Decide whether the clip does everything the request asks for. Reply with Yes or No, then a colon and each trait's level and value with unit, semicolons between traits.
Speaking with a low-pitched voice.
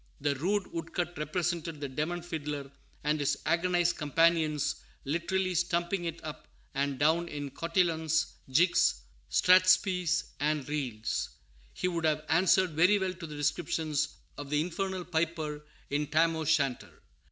No: medium, 160 Hz